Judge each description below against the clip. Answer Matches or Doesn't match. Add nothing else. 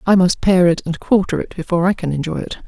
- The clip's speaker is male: Doesn't match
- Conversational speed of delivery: Doesn't match